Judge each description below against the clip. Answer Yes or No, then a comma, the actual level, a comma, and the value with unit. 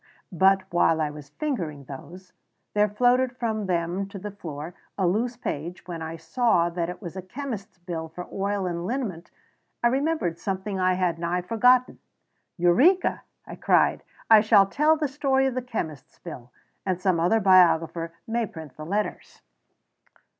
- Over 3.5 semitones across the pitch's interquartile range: Yes, average, 5.2 semitones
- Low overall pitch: No, high, 190 Hz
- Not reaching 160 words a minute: No, average, 170 wpm